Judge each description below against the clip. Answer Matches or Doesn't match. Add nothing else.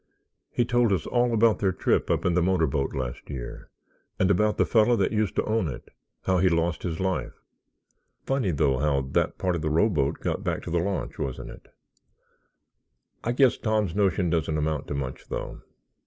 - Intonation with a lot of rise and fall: Matches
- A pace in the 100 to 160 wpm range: Doesn't match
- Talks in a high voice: Doesn't match